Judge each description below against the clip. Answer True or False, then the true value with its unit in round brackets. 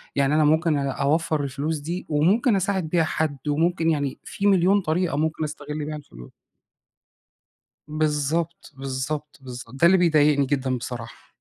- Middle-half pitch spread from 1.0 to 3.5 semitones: True (3.0 semitones)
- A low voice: False (155 Hz)